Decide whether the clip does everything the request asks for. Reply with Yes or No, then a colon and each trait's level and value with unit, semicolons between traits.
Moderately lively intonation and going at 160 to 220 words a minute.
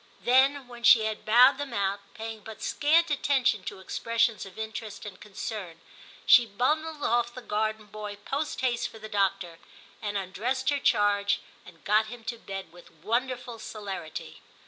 Yes: average, 3.5 semitones; average, 170 wpm